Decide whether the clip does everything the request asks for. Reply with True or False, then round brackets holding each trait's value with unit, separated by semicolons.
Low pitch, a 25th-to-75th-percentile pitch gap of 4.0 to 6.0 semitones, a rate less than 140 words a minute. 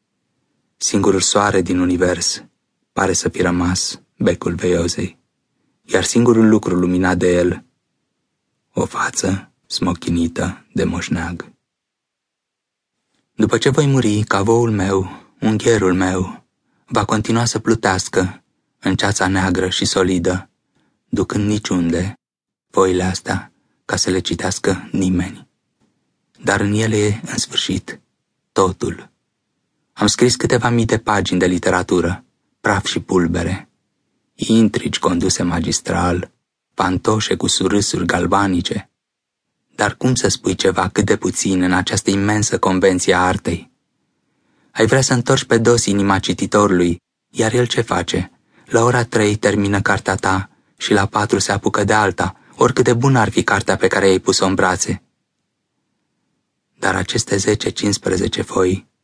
False (100 Hz; 3.1 semitones; 130 wpm)